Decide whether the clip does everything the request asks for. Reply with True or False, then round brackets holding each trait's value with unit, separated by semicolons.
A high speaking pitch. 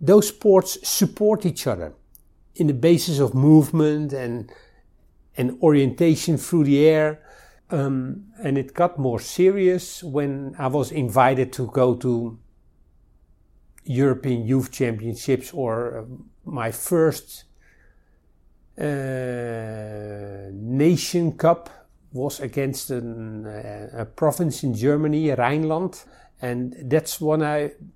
False (135 Hz)